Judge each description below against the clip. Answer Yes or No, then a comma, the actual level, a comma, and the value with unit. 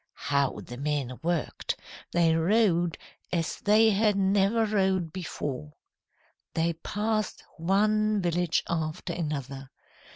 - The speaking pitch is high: No, medium, 175 Hz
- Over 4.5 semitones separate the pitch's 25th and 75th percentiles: Yes, average, 4.9 semitones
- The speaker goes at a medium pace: No, slow, 105 wpm